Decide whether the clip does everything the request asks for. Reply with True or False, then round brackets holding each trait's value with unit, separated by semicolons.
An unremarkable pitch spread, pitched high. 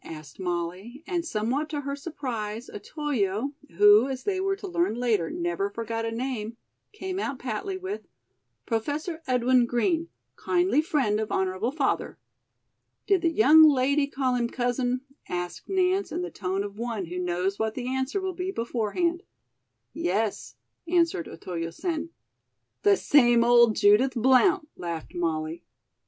False (7.4 semitones; 245 Hz)